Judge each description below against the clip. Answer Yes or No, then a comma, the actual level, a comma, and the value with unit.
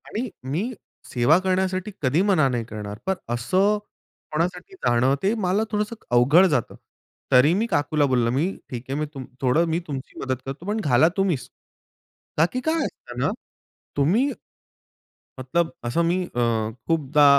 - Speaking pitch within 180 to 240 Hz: No, medium, 155 Hz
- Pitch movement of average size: No, wide, 6.4 semitones